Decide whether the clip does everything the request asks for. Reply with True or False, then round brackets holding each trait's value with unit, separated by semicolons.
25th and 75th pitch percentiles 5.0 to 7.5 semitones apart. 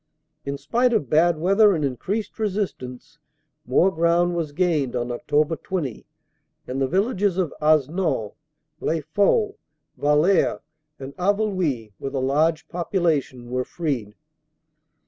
True (5.6 semitones)